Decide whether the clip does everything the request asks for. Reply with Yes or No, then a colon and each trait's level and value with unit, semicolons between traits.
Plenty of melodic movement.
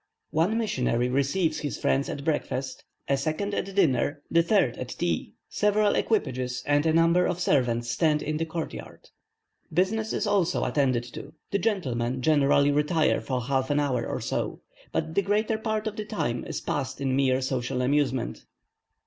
Yes: wide, 6.0 semitones